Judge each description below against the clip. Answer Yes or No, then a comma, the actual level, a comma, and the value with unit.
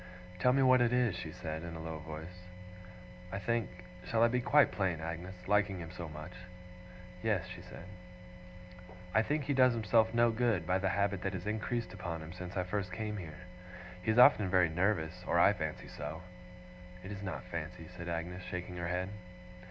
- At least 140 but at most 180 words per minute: No, average, 195 wpm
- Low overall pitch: Yes, very low, 95 Hz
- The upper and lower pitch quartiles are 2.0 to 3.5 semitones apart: No, average, 4.4 semitones